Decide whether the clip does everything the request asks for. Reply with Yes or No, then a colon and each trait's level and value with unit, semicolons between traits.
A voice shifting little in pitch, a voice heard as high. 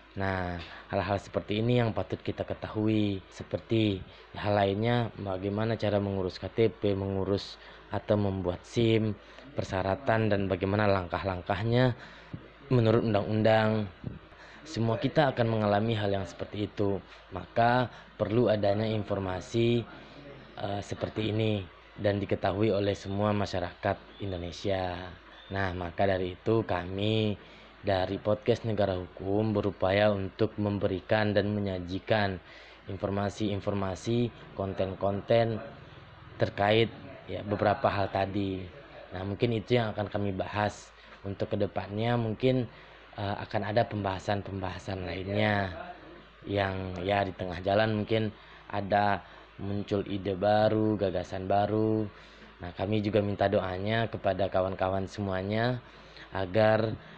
No: narrow, 2.3 semitones; low, 100 Hz